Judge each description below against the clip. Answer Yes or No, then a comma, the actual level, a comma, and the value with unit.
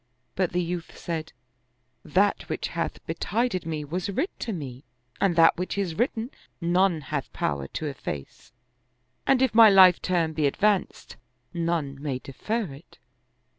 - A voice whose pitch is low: No, medium, 170 Hz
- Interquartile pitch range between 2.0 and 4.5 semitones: No, average, 4.9 semitones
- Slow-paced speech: No, average, 155 wpm